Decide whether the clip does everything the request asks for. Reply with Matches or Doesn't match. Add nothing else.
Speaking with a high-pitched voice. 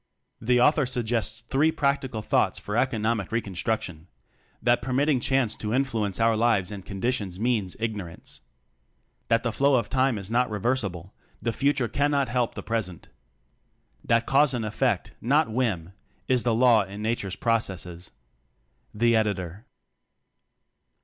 Doesn't match